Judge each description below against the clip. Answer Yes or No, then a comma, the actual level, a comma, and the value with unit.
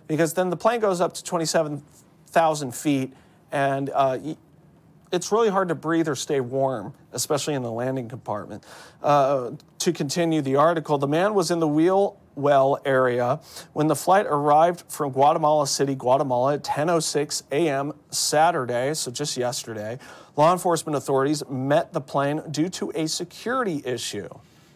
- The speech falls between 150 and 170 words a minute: Yes, average, 155 wpm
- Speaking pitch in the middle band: Yes, medium, 150 Hz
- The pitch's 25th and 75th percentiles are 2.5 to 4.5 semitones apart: Yes, average, 3.4 semitones